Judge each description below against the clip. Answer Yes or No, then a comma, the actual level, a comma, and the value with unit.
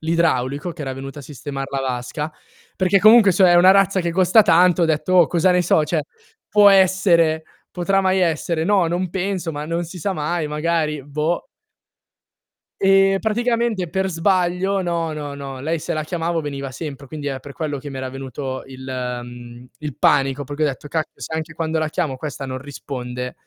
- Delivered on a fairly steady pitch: No, average, 4.5 semitones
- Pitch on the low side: No, medium, 160 Hz